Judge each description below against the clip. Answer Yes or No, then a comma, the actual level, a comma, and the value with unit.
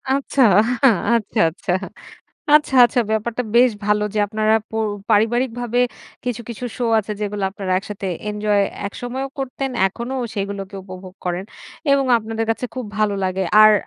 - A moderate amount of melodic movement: Yes, average, 3.4 semitones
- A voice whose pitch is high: Yes, high, 215 Hz